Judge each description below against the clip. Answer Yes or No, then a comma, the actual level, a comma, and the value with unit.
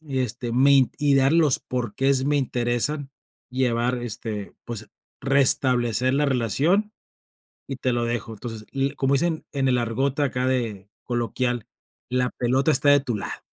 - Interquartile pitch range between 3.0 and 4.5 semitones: No, narrow, 2.6 semitones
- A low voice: Yes, low, 130 Hz